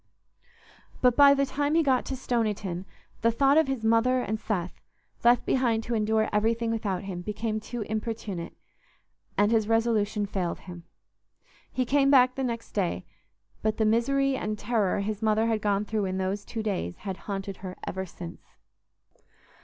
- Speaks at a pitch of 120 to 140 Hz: No, high, 220 Hz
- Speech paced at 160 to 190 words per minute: Yes, average, 170 wpm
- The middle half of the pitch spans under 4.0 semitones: Yes, average, 3.3 semitones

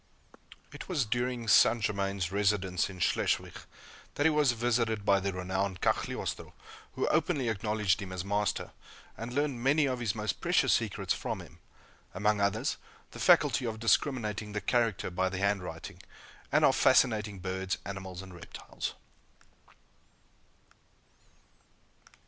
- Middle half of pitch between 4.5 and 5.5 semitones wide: No, average, 3.8 semitones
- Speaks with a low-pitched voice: Yes, low, 105 Hz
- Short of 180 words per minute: Yes, slow, 135 wpm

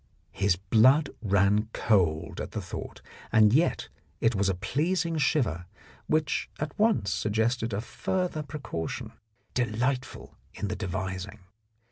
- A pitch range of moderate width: No, wide, 6.6 semitones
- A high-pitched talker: No, low, 110 Hz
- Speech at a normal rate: No, slow, 125 wpm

